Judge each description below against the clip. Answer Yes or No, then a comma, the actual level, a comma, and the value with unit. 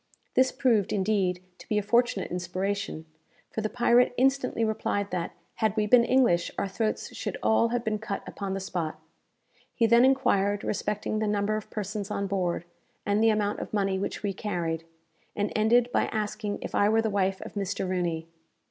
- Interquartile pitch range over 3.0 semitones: No, narrow, 2.5 semitones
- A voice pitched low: No, high, 210 Hz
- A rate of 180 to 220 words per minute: Yes, average, 185 wpm